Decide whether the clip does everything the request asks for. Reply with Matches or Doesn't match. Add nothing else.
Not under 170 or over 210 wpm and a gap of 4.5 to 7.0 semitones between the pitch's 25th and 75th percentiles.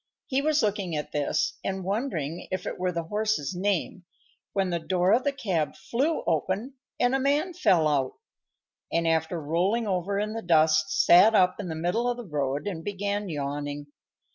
Matches